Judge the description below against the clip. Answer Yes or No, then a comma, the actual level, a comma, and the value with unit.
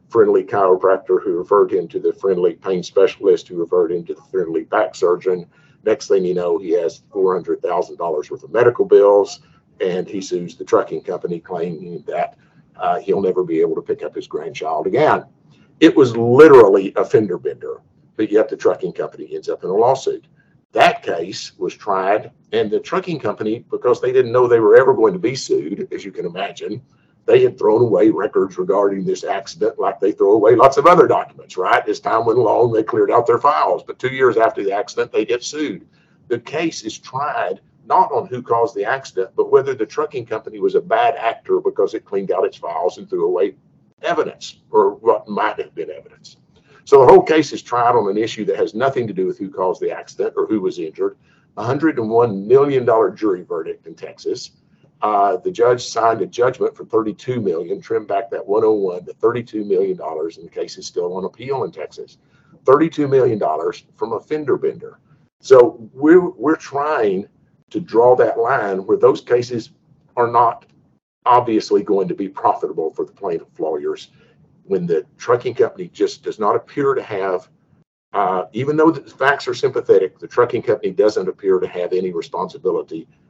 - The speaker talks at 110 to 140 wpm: No, average, 195 wpm